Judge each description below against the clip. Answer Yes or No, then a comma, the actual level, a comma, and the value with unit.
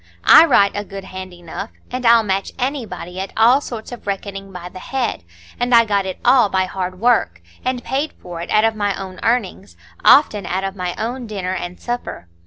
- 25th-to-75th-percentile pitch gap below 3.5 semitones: No, average, 4.3 semitones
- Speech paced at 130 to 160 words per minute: No, average, 200 wpm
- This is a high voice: Yes, high, 200 Hz